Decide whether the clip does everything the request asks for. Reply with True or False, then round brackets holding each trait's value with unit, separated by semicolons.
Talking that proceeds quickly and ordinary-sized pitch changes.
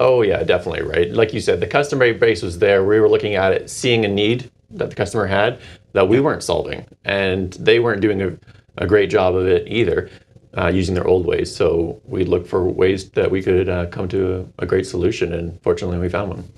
False (230 wpm; 6.3 semitones)